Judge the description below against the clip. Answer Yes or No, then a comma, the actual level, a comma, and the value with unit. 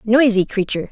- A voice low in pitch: No, high, 220 Hz